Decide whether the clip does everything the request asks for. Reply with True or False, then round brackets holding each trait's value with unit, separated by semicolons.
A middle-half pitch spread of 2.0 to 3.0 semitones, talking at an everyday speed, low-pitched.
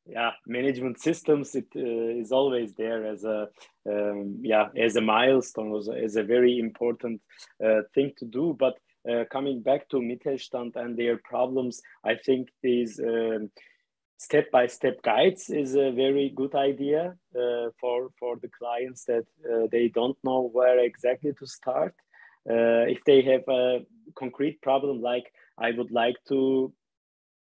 True (2.4 semitones; 160 wpm; 125 Hz)